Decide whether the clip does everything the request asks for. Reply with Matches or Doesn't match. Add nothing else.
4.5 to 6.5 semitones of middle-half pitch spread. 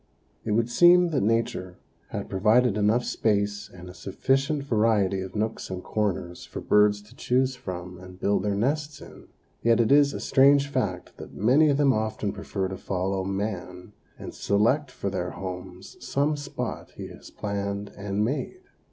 Matches